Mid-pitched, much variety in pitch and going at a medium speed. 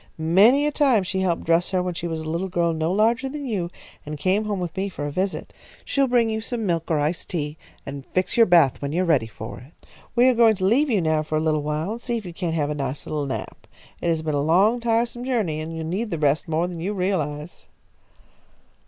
No: medium, 175 Hz; wide, 5.7 semitones; fast, 255 wpm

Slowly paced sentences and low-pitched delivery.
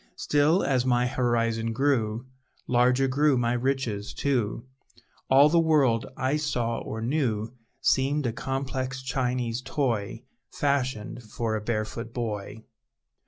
Yes: slow, 120 wpm; low, 125 Hz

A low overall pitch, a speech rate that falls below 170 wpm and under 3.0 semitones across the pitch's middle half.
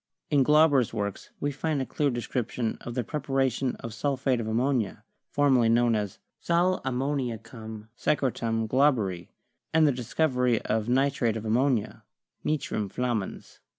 No: low, 125 Hz; average, 140 wpm; average, 3.8 semitones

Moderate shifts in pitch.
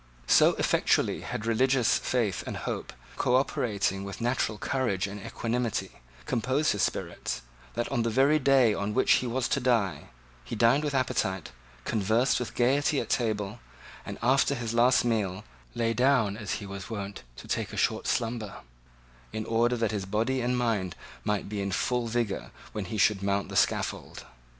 Yes: average, 3.5 semitones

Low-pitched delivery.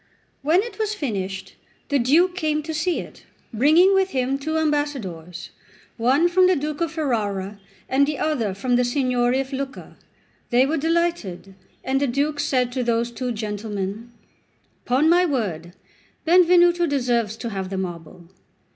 No: very high, 265 Hz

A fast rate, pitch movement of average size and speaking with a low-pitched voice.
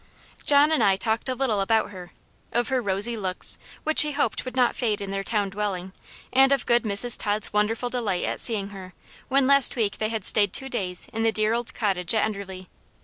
No: fast, 215 wpm; average, 3.7 semitones; high, 215 Hz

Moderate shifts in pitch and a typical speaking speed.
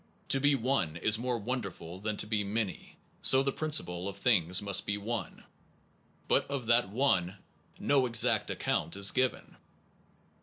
Yes: average, 4.5 semitones; average, 165 wpm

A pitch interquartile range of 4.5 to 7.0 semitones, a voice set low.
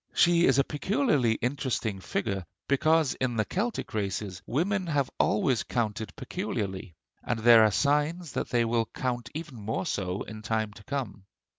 Yes: wide, 5.5 semitones; low, 120 Hz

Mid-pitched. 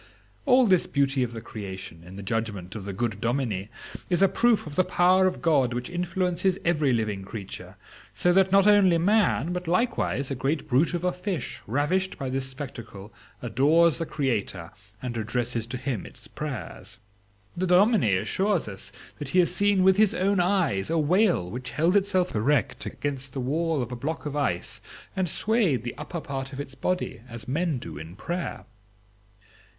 Yes: medium, 145 Hz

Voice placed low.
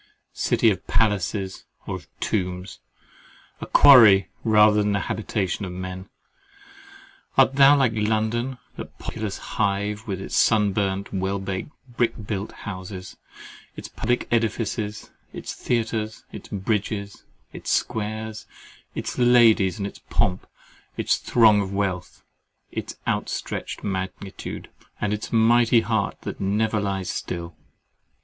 Yes: low, 105 Hz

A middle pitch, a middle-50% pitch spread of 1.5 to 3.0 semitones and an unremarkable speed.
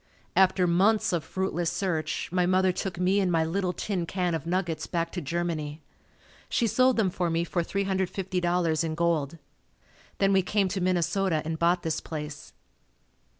Yes: medium, 175 Hz; narrow, 2.4 semitones; average, 165 wpm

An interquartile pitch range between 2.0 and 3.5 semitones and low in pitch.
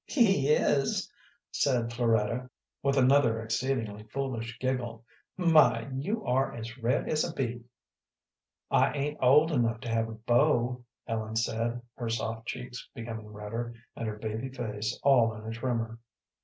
Yes: average, 2.8 semitones; low, 120 Hz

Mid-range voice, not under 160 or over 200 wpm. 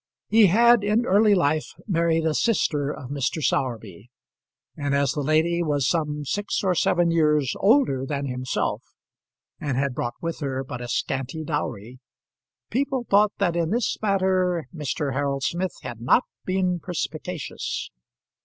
No: medium, 160 Hz; average, 150 wpm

